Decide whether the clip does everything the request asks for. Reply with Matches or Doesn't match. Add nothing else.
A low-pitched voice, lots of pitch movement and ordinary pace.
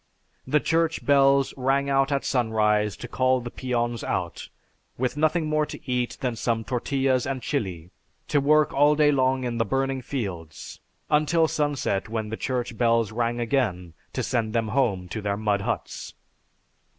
Doesn't match